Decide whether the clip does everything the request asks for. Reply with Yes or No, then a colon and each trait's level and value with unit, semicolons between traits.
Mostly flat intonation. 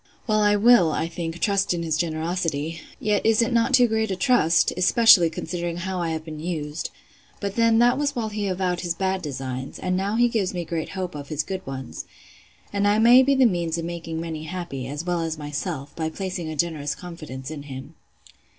No: average, 4.3 semitones